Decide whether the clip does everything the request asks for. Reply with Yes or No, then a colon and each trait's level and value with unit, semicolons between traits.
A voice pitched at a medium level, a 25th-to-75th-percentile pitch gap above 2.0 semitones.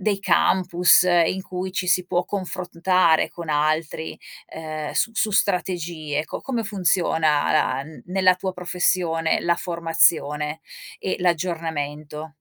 Yes: medium, 170 Hz; average, 2.7 semitones